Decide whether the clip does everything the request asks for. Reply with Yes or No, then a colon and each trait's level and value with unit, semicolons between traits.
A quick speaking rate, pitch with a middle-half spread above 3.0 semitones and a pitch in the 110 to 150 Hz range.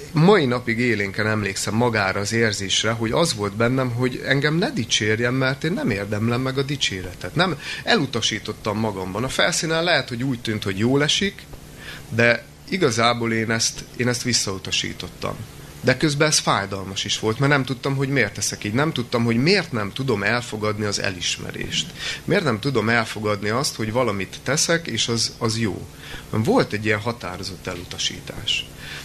Yes: fast, 165 wpm; average, 4.3 semitones; low, 115 Hz